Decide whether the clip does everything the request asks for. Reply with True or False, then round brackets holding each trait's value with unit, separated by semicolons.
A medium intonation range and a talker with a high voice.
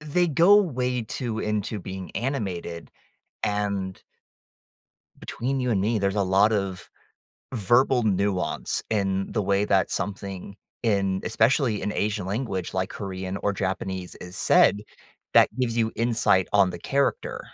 False (3.5 semitones; 105 Hz)